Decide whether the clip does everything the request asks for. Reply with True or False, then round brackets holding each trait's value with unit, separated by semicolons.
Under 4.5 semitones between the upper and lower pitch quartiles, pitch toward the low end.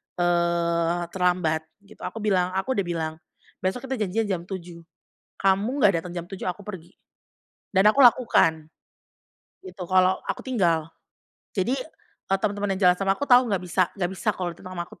False (2.9 semitones; 185 Hz)